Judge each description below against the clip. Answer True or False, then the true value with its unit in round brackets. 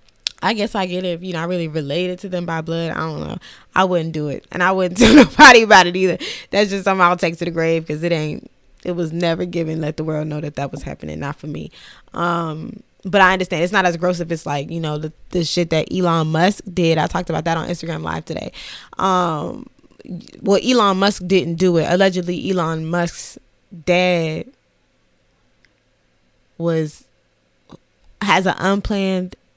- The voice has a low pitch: False (175 Hz)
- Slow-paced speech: False (200 wpm)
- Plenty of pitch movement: False (2.4 semitones)